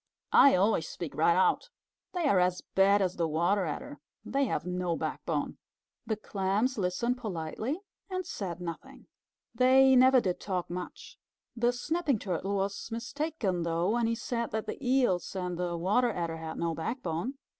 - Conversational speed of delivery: Yes, average, 165 wpm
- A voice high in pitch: Yes, high, 195 Hz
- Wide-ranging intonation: Yes, wide, 5.8 semitones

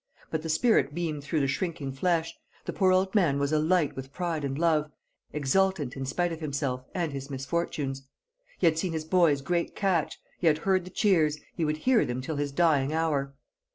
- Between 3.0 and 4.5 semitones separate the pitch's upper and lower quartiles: Yes, average, 3.8 semitones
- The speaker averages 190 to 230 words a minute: Yes, average, 200 wpm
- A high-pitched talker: No, medium, 155 Hz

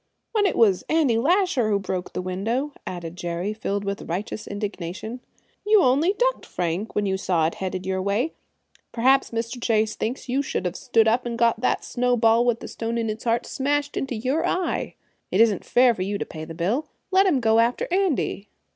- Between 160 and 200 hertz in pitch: No, high, 230 Hz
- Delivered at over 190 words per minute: Yes, average, 200 wpm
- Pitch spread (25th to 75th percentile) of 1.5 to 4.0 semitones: No, average, 4.9 semitones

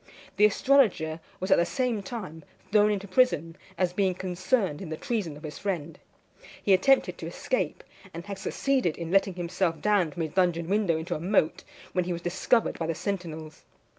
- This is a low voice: No, medium, 185 Hz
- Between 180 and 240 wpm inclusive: Yes, average, 190 wpm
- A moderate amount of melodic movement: Yes, average, 3.7 semitones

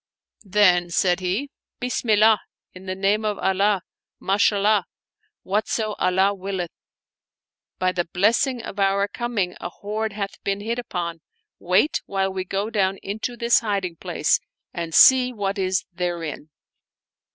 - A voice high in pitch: Yes, high, 195 Hz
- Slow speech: No, average, 150 wpm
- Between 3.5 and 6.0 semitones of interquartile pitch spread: No, narrow, 2.6 semitones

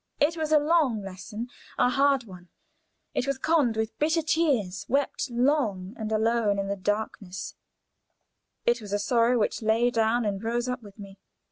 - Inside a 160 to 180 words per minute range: Yes, average, 170 wpm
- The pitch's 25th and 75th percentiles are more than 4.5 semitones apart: Yes, average, 5.0 semitones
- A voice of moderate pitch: No, high, 230 Hz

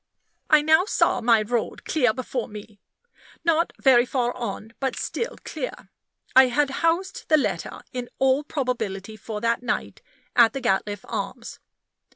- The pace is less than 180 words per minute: Yes, average, 150 wpm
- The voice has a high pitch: Yes, very high, 250 Hz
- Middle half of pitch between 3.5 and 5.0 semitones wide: Yes, average, 4.6 semitones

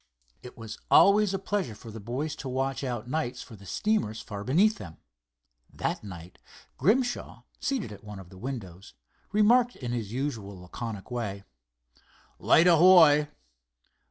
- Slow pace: No, average, 150 wpm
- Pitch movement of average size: No, wide, 9.0 semitones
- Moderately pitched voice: No, low, 125 Hz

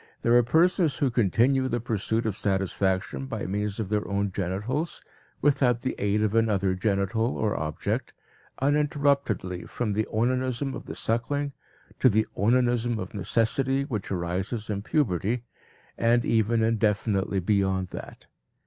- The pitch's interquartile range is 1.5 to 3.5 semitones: No, average, 4.1 semitones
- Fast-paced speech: No, average, 140 wpm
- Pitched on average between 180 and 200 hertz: No, low, 110 Hz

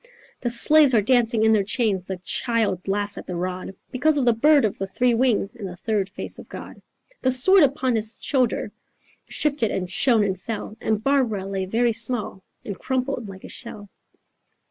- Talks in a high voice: Yes, high, 225 Hz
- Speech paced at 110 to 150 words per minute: No, average, 190 wpm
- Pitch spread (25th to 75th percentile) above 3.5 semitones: Yes, average, 4.4 semitones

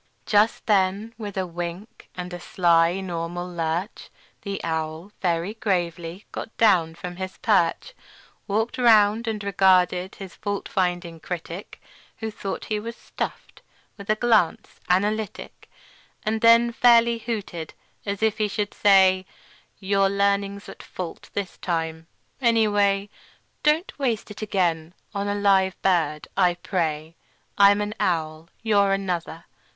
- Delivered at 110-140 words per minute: Yes, slow, 135 wpm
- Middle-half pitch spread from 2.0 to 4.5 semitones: Yes, average, 3.2 semitones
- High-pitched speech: Yes, high, 195 Hz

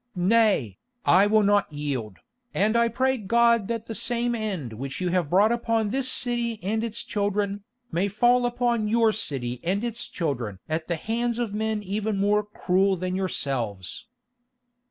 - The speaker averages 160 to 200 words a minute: Yes, average, 165 wpm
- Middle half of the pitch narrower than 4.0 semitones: No, average, 4.5 semitones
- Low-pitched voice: No, high, 205 Hz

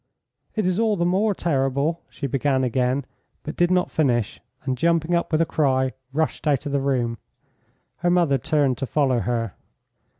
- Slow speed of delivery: No, average, 180 wpm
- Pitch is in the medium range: Yes, medium, 145 Hz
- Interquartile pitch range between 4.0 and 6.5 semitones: Yes, average, 4.5 semitones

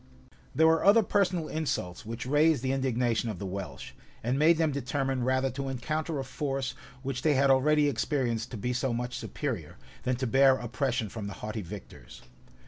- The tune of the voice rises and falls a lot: No, average, 3.7 semitones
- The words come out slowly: No, average, 185 wpm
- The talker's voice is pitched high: No, low, 130 Hz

